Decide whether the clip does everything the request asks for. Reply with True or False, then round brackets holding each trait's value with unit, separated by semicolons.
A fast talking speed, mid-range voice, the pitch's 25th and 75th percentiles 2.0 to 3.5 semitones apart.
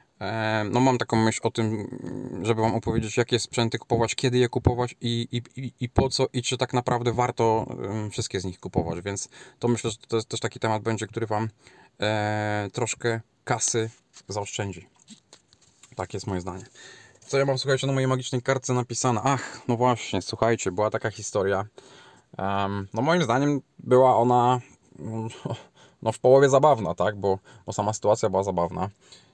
False (170 wpm; 115 Hz; 3.0 semitones)